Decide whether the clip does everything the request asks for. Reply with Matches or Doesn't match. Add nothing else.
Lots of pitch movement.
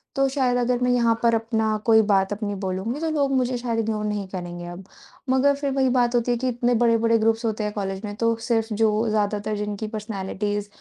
Doesn't match